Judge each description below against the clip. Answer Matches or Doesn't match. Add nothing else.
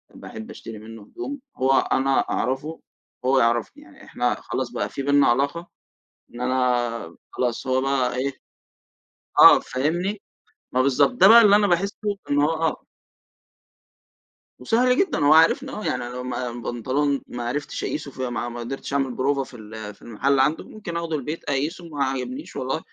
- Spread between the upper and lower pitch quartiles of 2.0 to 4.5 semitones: Doesn't match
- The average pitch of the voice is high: Doesn't match